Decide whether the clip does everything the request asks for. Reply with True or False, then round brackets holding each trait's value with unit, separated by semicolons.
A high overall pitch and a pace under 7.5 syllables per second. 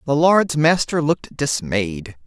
False (140 Hz; 3.9 syllables/s)